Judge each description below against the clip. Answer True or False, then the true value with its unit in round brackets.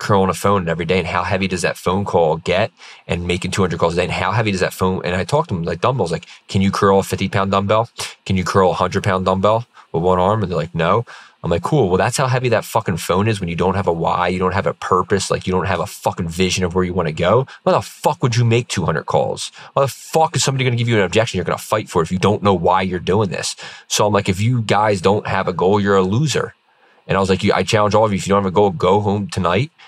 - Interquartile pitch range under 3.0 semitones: True (2.4 semitones)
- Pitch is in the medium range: False (95 Hz)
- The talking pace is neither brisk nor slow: False (305 wpm)